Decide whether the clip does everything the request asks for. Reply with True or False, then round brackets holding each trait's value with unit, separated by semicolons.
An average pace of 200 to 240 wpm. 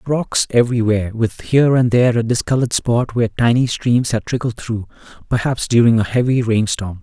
False (170 wpm)